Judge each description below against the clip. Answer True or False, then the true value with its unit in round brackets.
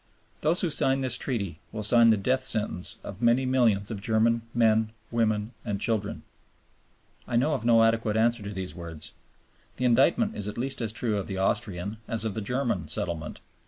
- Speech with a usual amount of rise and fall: True (3.1 semitones)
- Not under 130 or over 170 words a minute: False (190 wpm)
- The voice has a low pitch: True (115 Hz)